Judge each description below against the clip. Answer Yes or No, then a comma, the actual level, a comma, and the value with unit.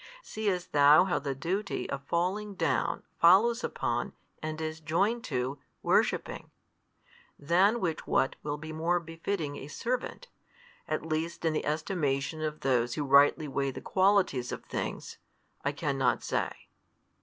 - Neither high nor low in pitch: Yes, medium, 155 Hz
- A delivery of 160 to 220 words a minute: No, average, 145 wpm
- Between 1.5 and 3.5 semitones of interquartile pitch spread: No, average, 4.3 semitones